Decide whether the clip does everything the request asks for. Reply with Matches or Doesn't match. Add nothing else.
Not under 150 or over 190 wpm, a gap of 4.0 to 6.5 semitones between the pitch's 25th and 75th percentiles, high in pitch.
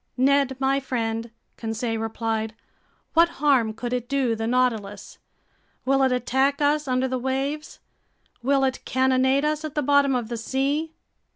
Doesn't match